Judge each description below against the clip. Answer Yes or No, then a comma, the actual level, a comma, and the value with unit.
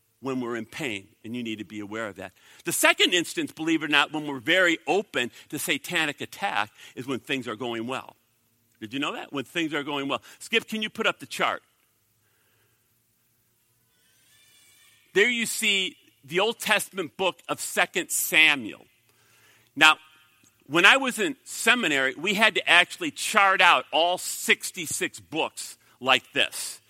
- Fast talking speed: No, average, 165 wpm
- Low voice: No, medium, 150 Hz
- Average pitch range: No, wide, 8.9 semitones